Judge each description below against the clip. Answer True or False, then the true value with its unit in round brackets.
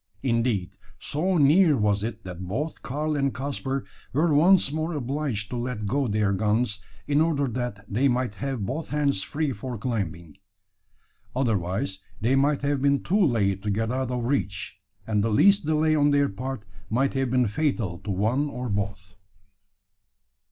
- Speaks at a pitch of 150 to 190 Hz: False (125 Hz)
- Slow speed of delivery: False (165 wpm)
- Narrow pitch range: False (5.5 semitones)